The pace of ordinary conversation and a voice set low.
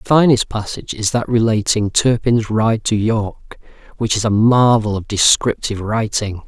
Yes: average, 160 wpm; low, 110 Hz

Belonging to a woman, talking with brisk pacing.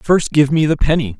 No: male; fast, 250 wpm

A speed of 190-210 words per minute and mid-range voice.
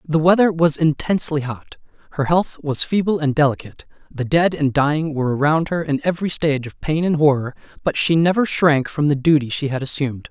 Yes: fast, 205 wpm; medium, 150 Hz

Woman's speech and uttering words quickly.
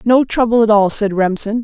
Yes: female; fast, 220 wpm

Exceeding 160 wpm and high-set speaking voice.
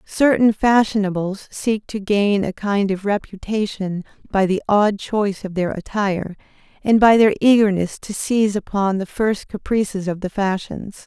No: average, 155 wpm; high, 200 Hz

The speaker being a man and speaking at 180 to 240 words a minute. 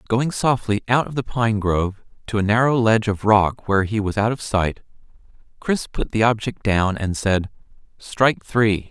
Yes: male; average, 190 wpm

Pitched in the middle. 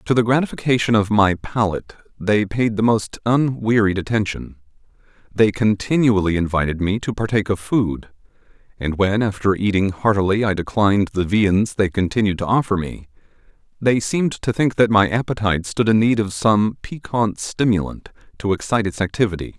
No: low, 105 Hz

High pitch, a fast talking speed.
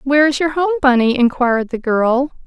No: very high, 270 Hz; average, 195 wpm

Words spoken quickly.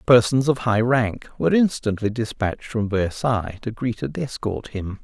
No: average, 165 wpm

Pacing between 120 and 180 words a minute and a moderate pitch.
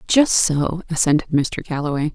Yes: average, 140 wpm; medium, 160 Hz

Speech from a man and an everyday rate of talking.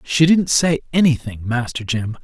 Yes: male; average, 160 wpm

